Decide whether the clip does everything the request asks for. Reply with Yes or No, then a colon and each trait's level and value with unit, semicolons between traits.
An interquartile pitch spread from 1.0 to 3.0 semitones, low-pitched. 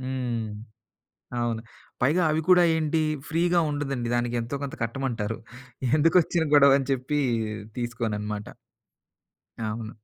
No: average, 4.3 semitones; low, 130 Hz